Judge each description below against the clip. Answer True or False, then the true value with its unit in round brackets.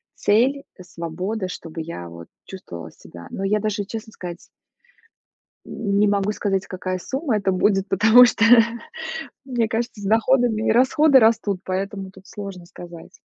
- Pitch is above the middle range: True (200 Hz)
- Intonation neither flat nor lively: True (3.3 semitones)